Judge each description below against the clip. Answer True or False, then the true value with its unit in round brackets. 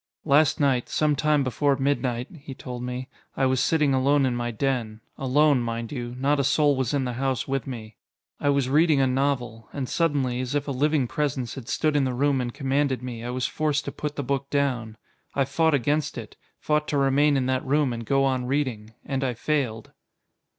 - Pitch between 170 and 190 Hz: False (135 Hz)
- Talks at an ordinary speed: False (215 wpm)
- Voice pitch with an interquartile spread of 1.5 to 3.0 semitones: True (2.4 semitones)